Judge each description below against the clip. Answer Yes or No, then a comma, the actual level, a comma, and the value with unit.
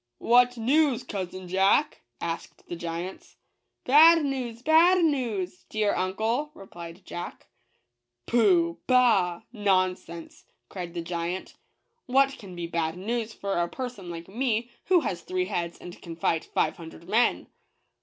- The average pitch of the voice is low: No, high, 195 Hz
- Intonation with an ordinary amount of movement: No, wide, 6.2 semitones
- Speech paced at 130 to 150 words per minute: No, average, 160 wpm